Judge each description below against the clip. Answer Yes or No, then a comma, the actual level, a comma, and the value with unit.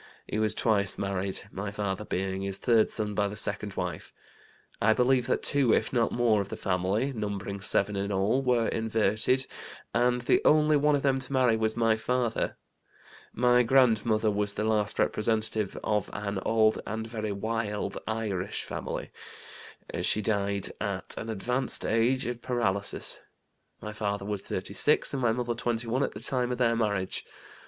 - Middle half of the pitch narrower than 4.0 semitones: Yes, average, 3.1 semitones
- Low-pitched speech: Yes, low, 110 Hz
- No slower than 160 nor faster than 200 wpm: Yes, average, 165 wpm